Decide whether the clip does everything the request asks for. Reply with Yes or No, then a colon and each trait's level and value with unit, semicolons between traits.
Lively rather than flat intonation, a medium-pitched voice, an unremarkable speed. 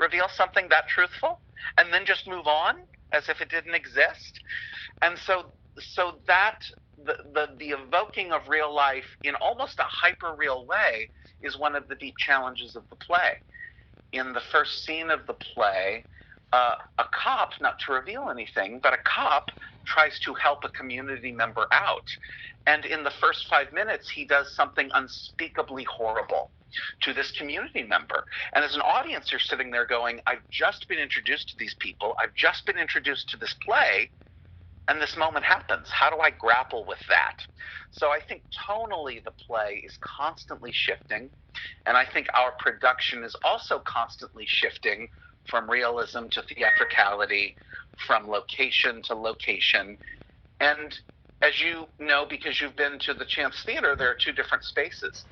Yes: wide, 6.8 semitones; medium, 155 Hz; average, 165 wpm